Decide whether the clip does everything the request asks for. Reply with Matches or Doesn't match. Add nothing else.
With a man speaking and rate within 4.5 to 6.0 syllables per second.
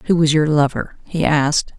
Doesn't match